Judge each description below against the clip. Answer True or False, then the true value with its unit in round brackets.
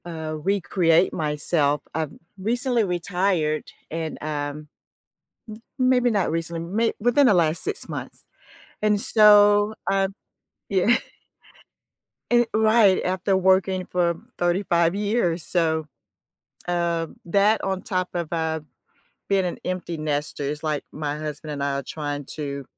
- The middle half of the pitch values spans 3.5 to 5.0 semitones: True (4.3 semitones)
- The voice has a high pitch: False (175 Hz)